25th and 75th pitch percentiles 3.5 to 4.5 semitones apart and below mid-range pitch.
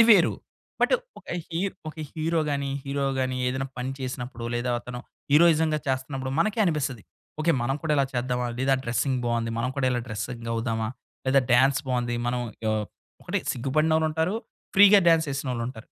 Yes: average, 4.1 semitones; low, 130 Hz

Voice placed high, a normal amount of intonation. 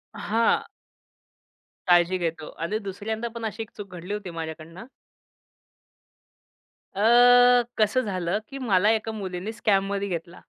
Yes: high, 195 Hz; average, 3.5 semitones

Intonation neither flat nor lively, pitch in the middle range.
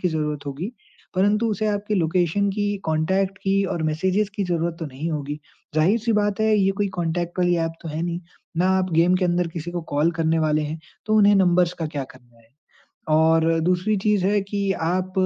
Yes: average, 3.8 semitones; medium, 175 Hz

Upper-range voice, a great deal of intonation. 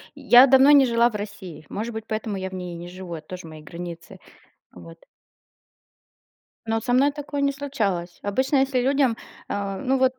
Yes: high, 220 Hz; wide, 6.6 semitones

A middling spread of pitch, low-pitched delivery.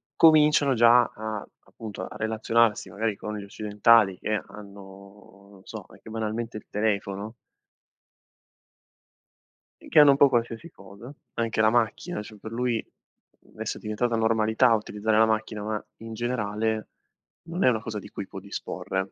No: narrow, 1.9 semitones; low, 110 Hz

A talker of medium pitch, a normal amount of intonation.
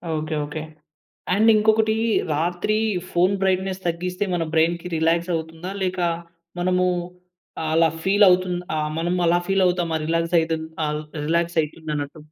No: medium, 175 Hz; narrow, 2.2 semitones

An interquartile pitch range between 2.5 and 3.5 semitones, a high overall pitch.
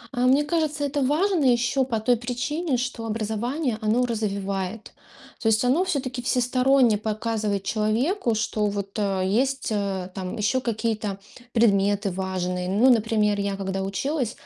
No: average, 4.0 semitones; high, 225 Hz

